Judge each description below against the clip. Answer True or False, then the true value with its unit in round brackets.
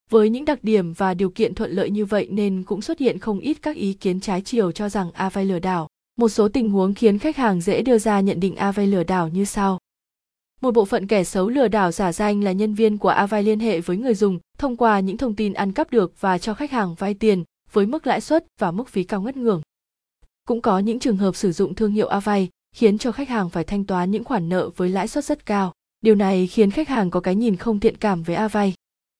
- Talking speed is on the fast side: True (255 wpm)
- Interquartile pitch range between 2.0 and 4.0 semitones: True (3.0 semitones)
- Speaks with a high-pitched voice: True (205 Hz)